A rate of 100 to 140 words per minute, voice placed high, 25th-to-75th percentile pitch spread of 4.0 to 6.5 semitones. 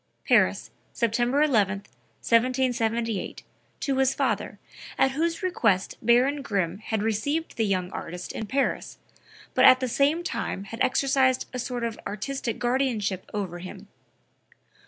Yes: slow, 135 wpm; high, 235 Hz; average, 4.5 semitones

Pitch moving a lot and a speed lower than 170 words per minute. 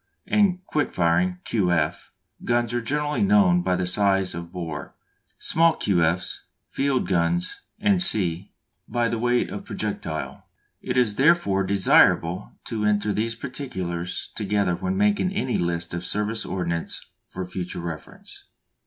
Yes: wide, 7.4 semitones; average, 140 wpm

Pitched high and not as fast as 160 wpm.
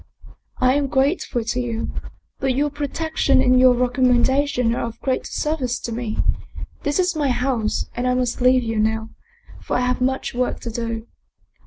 No: very high, 250 Hz; average, 175 wpm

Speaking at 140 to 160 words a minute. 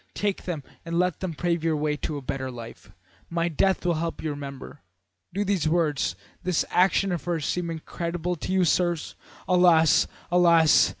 No: average, 180 wpm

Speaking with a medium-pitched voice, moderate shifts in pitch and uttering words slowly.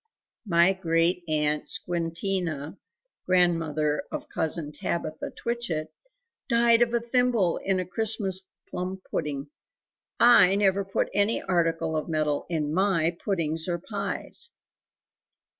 Yes: medium, 175 Hz; average, 3.7 semitones; slow, 115 wpm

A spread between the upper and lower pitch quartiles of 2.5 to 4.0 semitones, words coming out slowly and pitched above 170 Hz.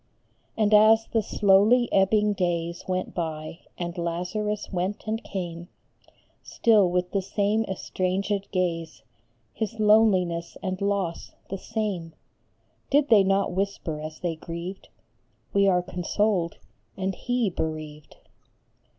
Yes: average, 3.4 semitones; slow, 125 wpm; high, 190 Hz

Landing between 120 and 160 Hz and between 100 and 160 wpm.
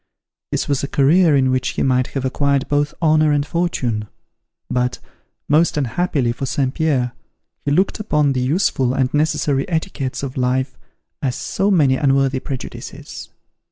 Yes: medium, 140 Hz; average, 155 wpm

